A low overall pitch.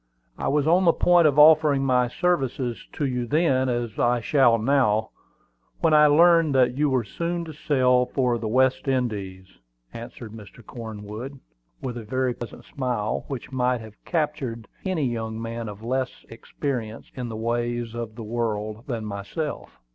Yes: low, 125 Hz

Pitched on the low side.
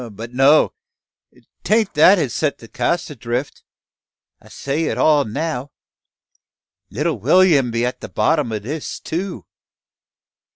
No: medium, 145 Hz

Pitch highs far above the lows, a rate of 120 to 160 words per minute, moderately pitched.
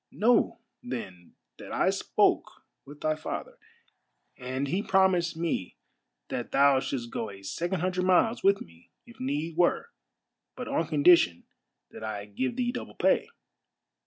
Yes: wide, 7.2 semitones; average, 150 wpm; medium, 160 Hz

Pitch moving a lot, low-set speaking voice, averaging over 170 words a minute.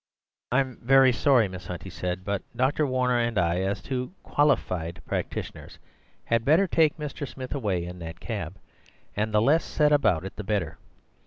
Yes: wide, 6.6 semitones; low, 115 Hz; average, 180 wpm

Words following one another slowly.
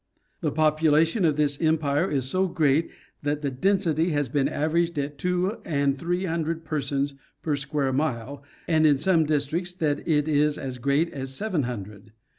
No: average, 170 wpm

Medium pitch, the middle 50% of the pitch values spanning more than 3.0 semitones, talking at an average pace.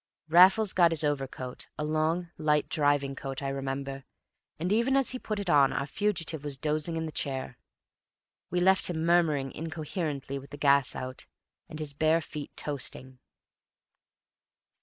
Yes: medium, 150 Hz; average, 3.6 semitones; average, 160 wpm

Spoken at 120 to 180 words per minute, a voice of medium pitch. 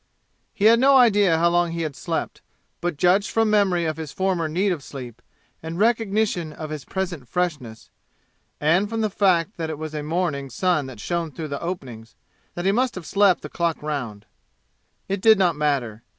No: average, 195 wpm; medium, 170 Hz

